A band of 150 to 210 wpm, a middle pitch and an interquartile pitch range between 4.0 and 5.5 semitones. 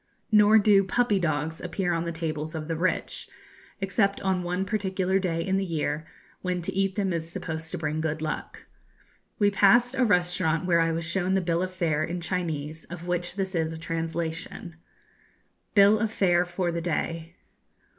No: average, 185 wpm; medium, 175 Hz; average, 2.8 semitones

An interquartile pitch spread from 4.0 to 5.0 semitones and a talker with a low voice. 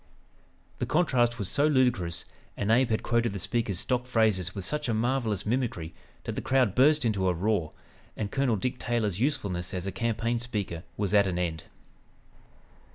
Yes: average, 4.6 semitones; low, 110 Hz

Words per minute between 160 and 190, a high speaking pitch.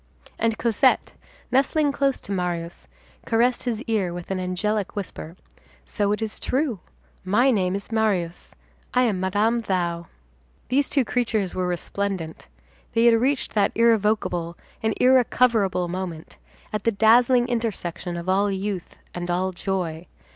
No: average, 140 wpm; high, 205 Hz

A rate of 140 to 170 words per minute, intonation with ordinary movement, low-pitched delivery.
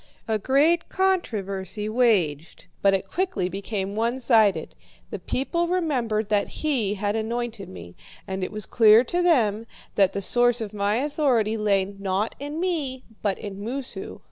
No: average, 155 wpm; average, 4.8 semitones; high, 220 Hz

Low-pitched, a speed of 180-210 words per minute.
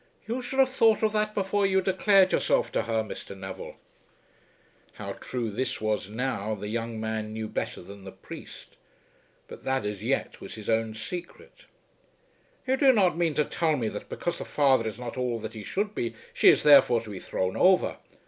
Yes: low, 125 Hz; average, 195 wpm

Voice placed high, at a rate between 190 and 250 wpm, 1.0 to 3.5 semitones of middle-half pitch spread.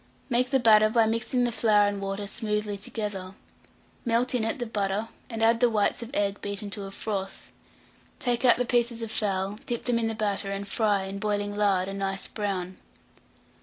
Yes: high, 210 Hz; average, 200 wpm; narrow, 2.6 semitones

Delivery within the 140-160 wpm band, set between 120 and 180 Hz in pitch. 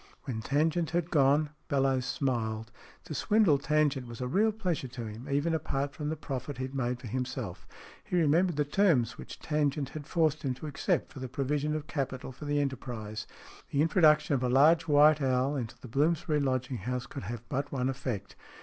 No: average, 195 wpm; medium, 140 Hz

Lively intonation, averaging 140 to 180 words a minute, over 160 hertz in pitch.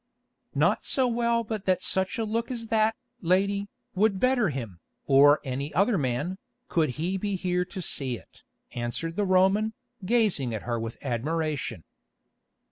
Yes: wide, 7.2 semitones; average, 155 wpm; medium, 185 Hz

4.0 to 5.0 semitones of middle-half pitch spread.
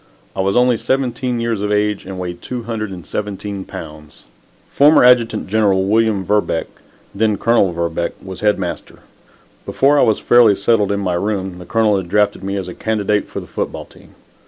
No: average, 3.0 semitones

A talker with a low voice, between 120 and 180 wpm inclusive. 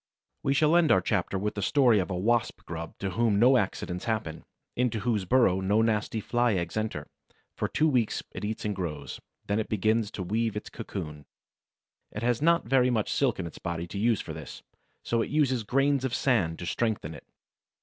No: low, 110 Hz; fast, 205 wpm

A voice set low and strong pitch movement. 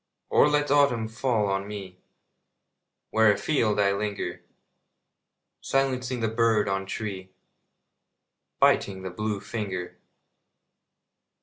No: low, 105 Hz; average, 3.2 semitones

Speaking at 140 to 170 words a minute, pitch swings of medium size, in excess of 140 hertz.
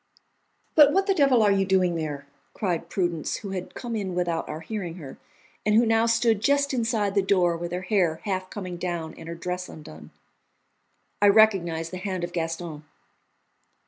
No: average, 180 wpm; average, 4.2 semitones; medium, 185 Hz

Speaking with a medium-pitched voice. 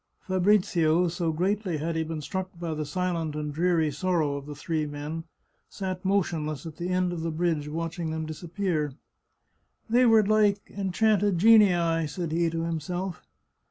Yes: medium, 170 Hz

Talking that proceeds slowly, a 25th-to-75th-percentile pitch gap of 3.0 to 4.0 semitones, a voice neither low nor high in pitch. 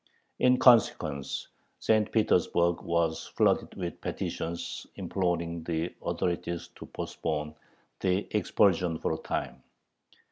No: slow, 105 wpm; average, 3.3 semitones; very low, 85 Hz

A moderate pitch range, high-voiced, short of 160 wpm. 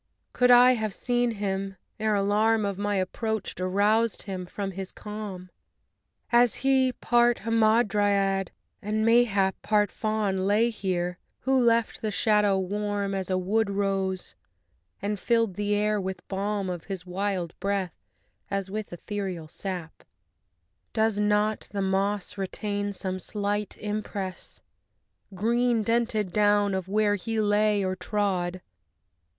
No: narrow, 2.1 semitones; high, 205 Hz; slow, 135 wpm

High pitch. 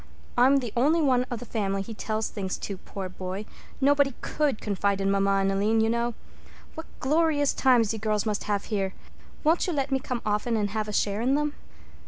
Yes: high, 225 Hz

